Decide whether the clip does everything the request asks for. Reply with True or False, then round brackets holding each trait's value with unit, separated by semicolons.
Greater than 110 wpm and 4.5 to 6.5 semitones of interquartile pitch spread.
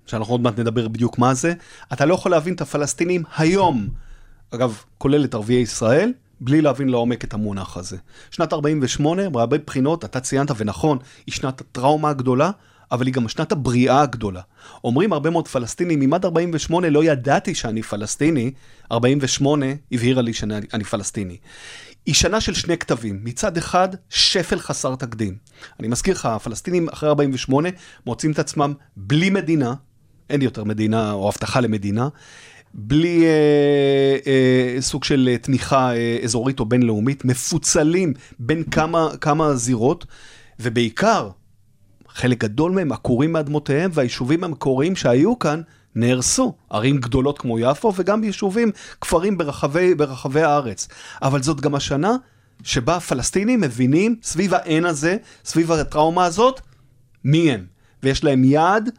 True (140 wpm; 4.9 semitones)